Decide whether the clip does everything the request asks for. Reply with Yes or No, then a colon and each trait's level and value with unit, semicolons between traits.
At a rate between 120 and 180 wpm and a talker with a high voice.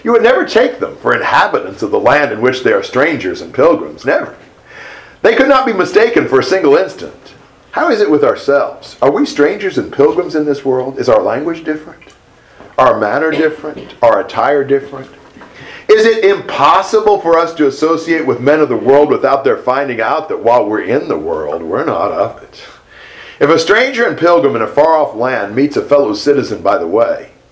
No: fast, 205 wpm; high, 195 Hz